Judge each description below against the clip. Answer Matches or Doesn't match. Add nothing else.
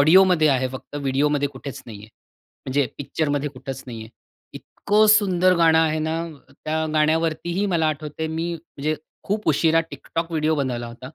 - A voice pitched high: Doesn't match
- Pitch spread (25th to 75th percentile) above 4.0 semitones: Doesn't match